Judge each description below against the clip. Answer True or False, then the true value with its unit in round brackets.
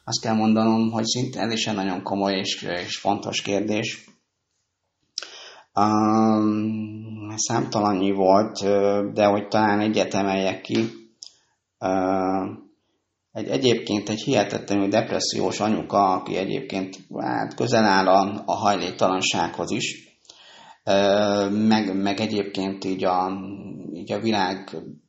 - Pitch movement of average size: False (2.1 semitones)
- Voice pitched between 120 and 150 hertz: False (100 Hz)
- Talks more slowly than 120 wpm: True (110 wpm)